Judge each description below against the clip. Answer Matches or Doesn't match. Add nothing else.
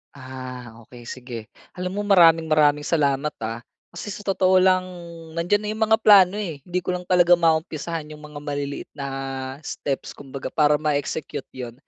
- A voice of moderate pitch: Matches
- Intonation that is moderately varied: Matches